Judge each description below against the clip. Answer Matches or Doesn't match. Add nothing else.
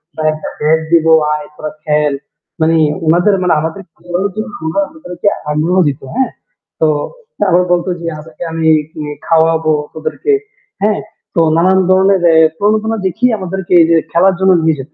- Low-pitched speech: Doesn't match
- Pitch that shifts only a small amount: Doesn't match